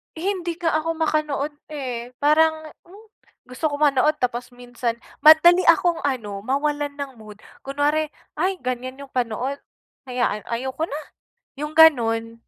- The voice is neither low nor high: No, very high, 285 Hz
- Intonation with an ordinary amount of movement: Yes, average, 4.2 semitones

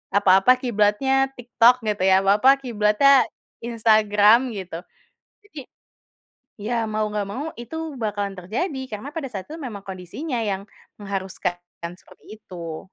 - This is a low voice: No, high, 215 Hz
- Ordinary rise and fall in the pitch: Yes, average, 4.1 semitones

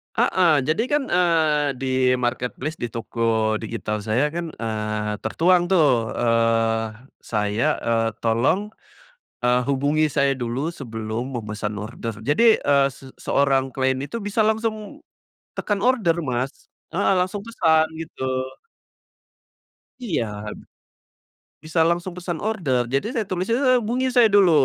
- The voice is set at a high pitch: No, medium, 140 Hz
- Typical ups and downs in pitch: No, wide, 7.7 semitones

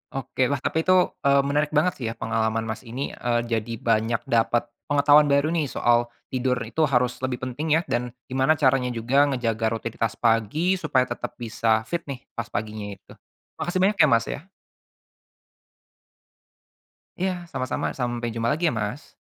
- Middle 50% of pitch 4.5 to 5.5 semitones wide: No, average, 4.1 semitones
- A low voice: Yes, low, 125 Hz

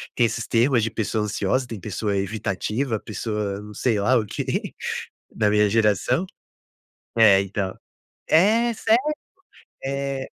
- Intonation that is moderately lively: Yes, average, 3.9 semitones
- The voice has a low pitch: Yes, low, 110 Hz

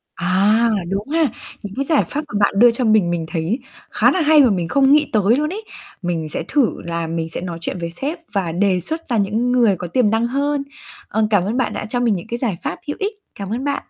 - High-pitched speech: Yes, high, 220 Hz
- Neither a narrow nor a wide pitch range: No, wide, 6.7 semitones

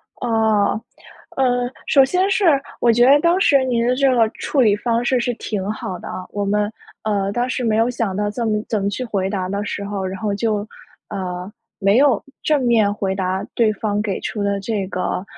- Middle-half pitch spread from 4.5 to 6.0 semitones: No, average, 3.4 semitones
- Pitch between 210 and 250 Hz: Yes, high, 215 Hz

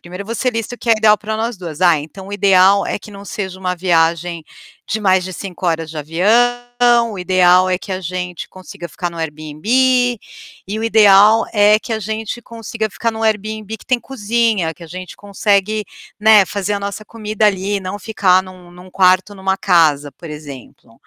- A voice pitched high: Yes, high, 195 Hz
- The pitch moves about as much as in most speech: Yes, average, 3.3 semitones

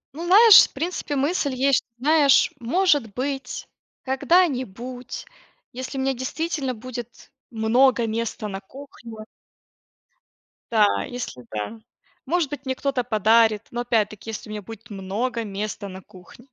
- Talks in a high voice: Yes, high, 245 Hz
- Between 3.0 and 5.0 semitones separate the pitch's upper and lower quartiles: Yes, average, 4.0 semitones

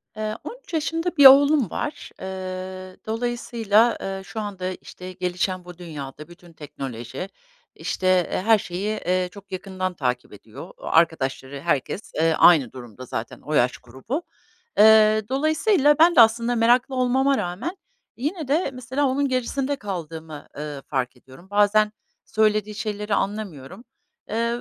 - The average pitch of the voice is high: Yes, high, 200 Hz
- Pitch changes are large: Yes, wide, 6.5 semitones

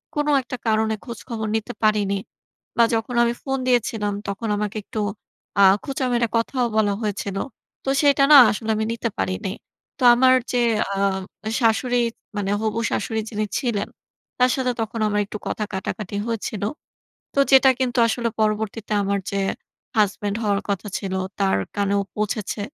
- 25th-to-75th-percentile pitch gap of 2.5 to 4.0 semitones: Yes, average, 2.9 semitones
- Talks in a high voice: Yes, high, 220 Hz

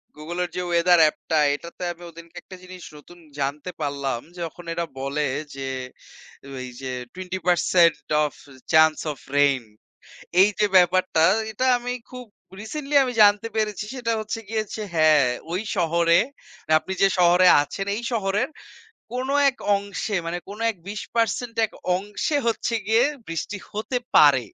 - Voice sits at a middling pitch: Yes, medium, 180 Hz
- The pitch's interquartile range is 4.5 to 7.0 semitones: Yes, average, 5.2 semitones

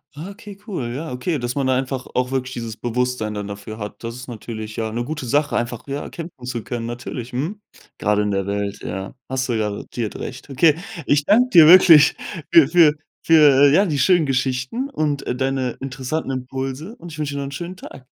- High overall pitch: No, low, 130 Hz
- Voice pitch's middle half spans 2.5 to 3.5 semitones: No, average, 4.2 semitones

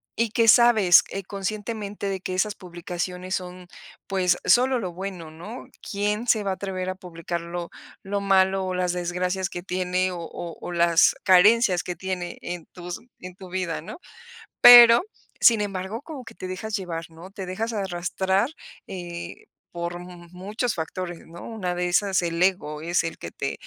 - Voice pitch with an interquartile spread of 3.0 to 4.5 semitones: No, narrow, 2.5 semitones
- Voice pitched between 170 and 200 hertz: Yes, medium, 185 Hz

